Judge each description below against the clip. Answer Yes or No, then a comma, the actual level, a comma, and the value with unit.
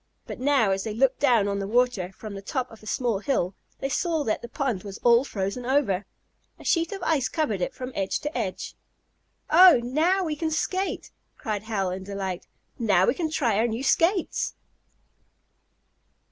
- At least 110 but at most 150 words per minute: No, average, 190 wpm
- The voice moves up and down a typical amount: No, wide, 6.8 semitones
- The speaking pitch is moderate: No, high, 240 Hz